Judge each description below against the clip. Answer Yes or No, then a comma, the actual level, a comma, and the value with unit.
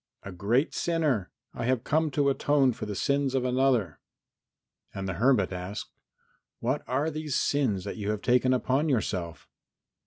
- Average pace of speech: Yes, average, 155 wpm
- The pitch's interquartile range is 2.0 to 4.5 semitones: No, wide, 5.5 semitones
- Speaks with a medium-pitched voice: No, low, 125 Hz